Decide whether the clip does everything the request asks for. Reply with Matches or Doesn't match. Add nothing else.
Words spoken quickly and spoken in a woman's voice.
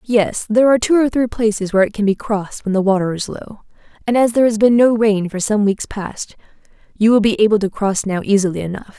Matches